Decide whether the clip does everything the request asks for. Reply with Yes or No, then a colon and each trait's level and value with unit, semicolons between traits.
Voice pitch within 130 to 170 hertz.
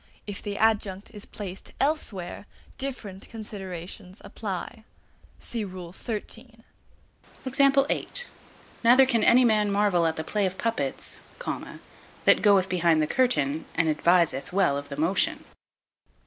No: high, 200 Hz